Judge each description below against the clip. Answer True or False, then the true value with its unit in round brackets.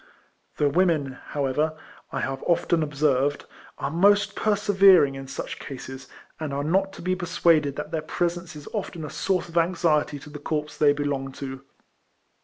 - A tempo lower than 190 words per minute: True (170 wpm)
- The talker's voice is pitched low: False (155 Hz)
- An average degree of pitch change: True (3.6 semitones)